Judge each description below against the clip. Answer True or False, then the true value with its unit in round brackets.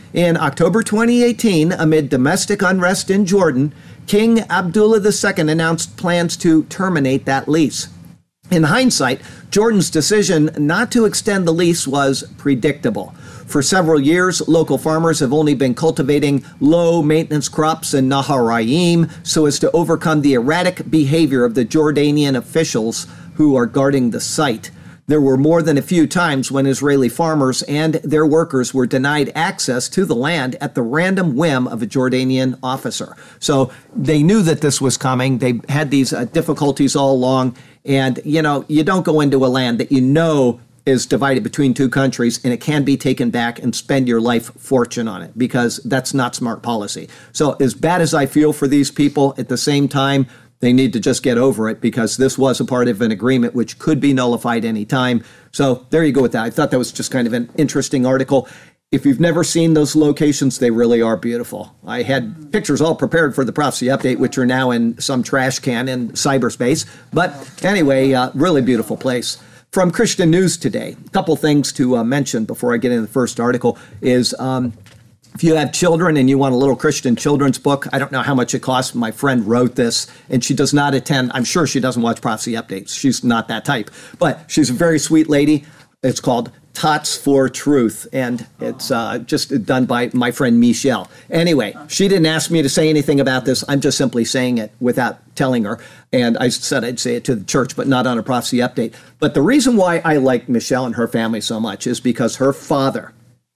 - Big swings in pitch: False (3.9 semitones)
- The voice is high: False (140 Hz)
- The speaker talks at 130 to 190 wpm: False (200 wpm)